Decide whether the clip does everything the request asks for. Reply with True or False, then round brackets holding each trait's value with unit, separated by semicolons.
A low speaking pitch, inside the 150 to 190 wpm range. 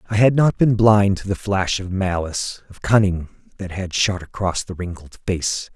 False (95 Hz; 200 wpm)